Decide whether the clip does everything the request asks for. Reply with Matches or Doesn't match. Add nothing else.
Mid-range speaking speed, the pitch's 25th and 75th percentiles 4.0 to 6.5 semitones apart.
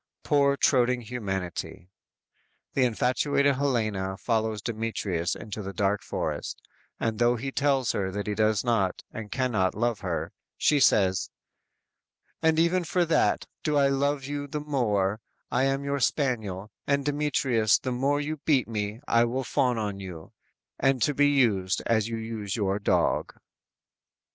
Matches